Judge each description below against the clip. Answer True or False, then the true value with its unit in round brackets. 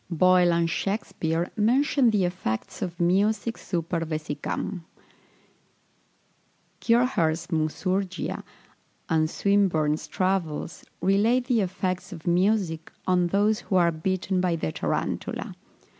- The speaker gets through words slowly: True (105 wpm)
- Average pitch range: True (3.3 semitones)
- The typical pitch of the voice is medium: True (180 Hz)